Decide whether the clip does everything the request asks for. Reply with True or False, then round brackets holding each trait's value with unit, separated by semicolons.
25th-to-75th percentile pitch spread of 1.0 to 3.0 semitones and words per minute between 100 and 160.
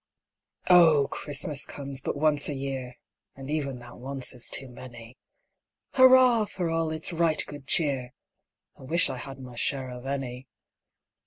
False (3.5 semitones; 155 wpm)